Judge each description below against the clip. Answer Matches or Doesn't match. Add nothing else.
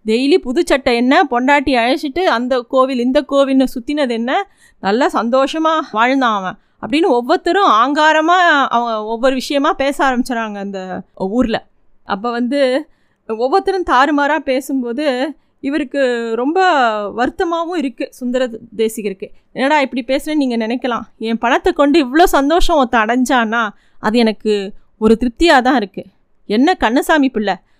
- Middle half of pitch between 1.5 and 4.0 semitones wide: Doesn't match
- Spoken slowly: Doesn't match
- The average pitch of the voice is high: Matches